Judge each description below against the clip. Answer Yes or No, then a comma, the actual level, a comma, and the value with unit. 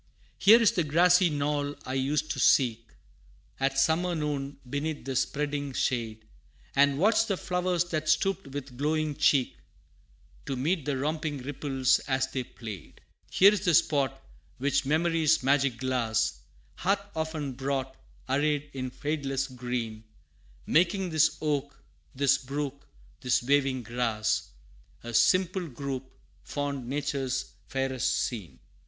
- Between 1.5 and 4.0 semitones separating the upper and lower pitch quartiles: Yes, average, 3.1 semitones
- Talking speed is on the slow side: Yes, slow, 130 wpm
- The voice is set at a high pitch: No, medium, 140 Hz